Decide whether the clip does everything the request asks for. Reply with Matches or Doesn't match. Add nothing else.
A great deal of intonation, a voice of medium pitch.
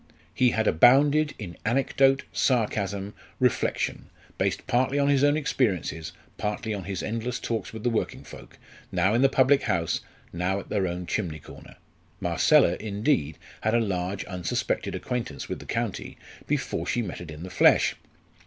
Doesn't match